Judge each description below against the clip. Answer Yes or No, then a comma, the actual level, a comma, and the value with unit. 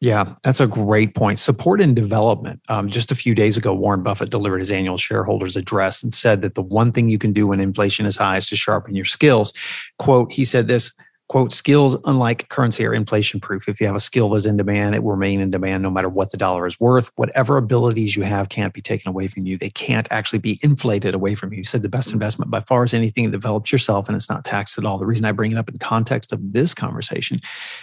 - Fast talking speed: Yes, fast, 250 wpm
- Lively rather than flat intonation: No, average, 3.4 semitones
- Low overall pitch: Yes, low, 110 Hz